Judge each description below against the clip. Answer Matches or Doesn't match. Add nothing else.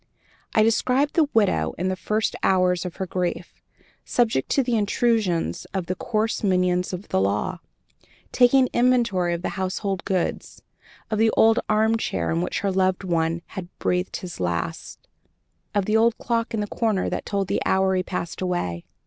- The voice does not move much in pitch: Doesn't match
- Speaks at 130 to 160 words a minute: Doesn't match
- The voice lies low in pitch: Doesn't match